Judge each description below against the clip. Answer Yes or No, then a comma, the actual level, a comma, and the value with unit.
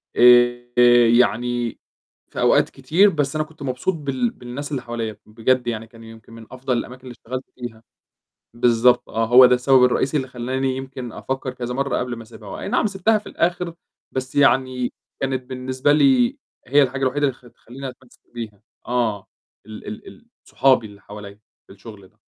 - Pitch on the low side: Yes, low, 125 Hz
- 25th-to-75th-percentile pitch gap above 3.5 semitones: No, narrow, 2.4 semitones